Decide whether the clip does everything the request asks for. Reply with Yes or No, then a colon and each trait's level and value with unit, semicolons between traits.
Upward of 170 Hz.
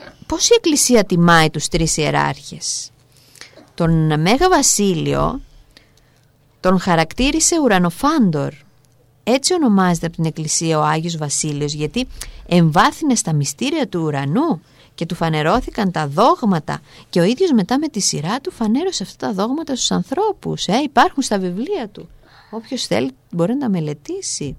Yes: medium, 185 Hz